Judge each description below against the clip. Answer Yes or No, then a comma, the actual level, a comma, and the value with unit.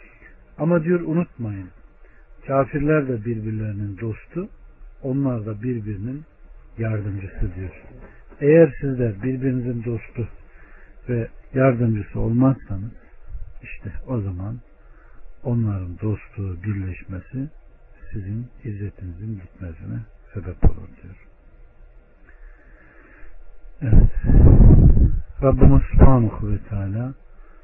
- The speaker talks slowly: Yes, slow, 75 wpm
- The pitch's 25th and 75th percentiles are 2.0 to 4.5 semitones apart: No, average, 5.1 semitones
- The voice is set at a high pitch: No, low, 110 Hz